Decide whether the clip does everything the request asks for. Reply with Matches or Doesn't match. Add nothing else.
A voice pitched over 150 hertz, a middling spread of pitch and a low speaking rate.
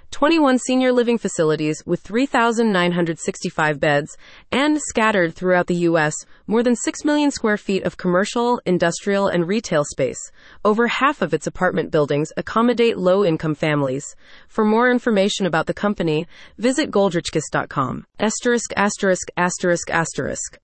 Doesn't match